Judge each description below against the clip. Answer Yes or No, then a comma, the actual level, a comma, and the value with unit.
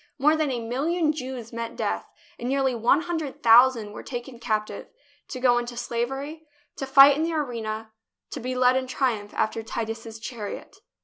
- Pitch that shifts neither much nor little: Yes, average, 3.1 semitones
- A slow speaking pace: No, average, 175 wpm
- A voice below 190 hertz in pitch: No, very high, 250 Hz